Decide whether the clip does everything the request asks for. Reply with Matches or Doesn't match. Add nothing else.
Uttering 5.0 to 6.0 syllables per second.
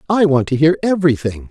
Doesn't match